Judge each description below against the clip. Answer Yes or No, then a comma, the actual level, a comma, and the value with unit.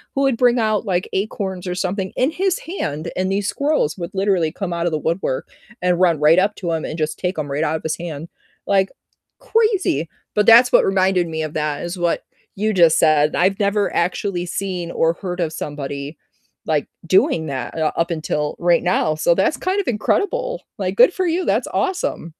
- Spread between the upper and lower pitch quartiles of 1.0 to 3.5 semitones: No, average, 4.7 semitones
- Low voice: No, medium, 180 Hz